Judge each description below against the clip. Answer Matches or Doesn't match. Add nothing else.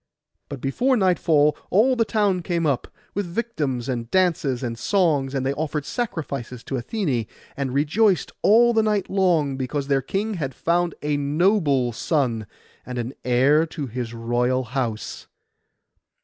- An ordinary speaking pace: Matches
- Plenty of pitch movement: Matches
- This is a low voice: Doesn't match